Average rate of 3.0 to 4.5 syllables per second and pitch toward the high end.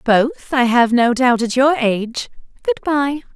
Yes: 4.0 syllables/s; high, 245 Hz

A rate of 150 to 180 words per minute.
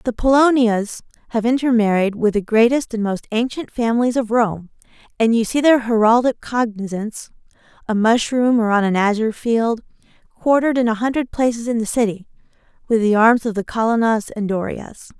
Yes: average, 165 wpm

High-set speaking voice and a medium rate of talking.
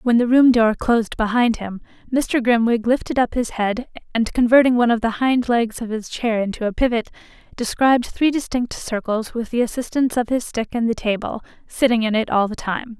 No: high, 235 Hz; fast, 210 wpm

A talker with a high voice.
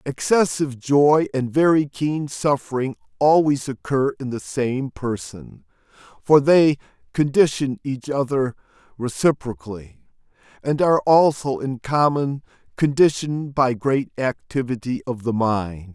No: low, 135 Hz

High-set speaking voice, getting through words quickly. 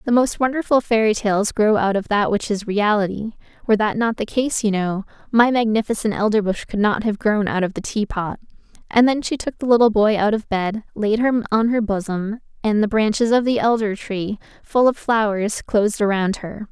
Yes: high, 215 Hz; fast, 210 wpm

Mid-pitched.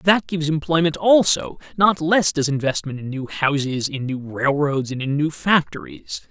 Yes: medium, 155 Hz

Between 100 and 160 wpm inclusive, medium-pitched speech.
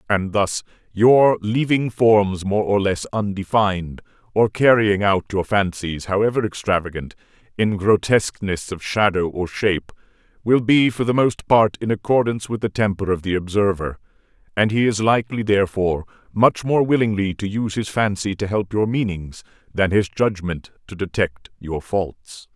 No: average, 155 wpm; low, 105 Hz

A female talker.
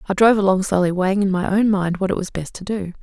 Yes: female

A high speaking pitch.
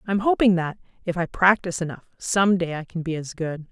No: medium, 180 Hz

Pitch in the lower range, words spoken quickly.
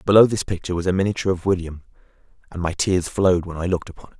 Yes: very low, 90 Hz; fast, 245 wpm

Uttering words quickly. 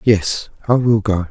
No: average, 185 wpm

